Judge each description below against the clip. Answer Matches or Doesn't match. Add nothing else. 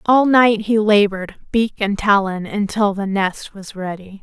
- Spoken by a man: Doesn't match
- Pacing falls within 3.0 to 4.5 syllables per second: Matches